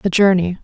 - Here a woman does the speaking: Yes, female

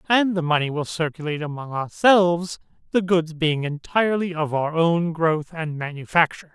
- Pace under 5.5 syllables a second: Yes, 5.1 syllables/s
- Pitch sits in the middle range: Yes, medium, 165 Hz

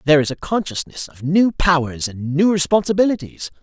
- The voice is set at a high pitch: No, medium, 160 Hz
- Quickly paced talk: No, average, 165 wpm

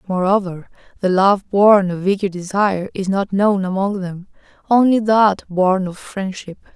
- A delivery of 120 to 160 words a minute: Yes, average, 150 wpm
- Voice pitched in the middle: No, high, 195 Hz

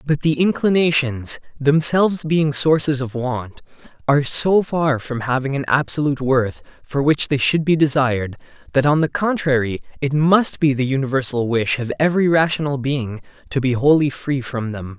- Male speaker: Yes, male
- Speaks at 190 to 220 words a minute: No, average, 170 wpm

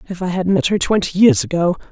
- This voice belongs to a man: No, female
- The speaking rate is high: Yes, fast, 250 wpm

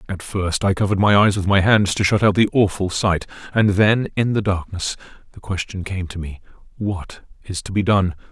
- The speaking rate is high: Yes, fast, 215 wpm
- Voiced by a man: Yes, male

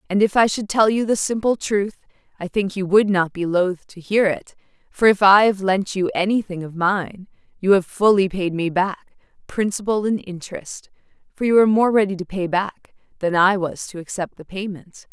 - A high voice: Yes, high, 195 Hz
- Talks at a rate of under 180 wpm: No, fast, 205 wpm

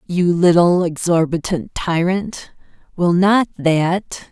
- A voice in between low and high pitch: Yes, medium, 175 Hz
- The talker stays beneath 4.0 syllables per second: Yes, 3.6 syllables/s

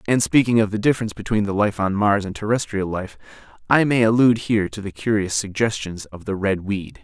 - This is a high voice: No, low, 105 Hz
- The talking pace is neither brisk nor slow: No, fast, 215 wpm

